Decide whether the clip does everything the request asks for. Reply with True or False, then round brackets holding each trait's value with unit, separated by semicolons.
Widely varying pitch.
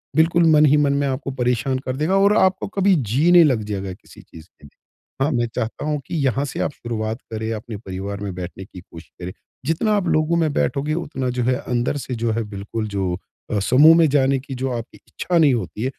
True (5.8 semitones)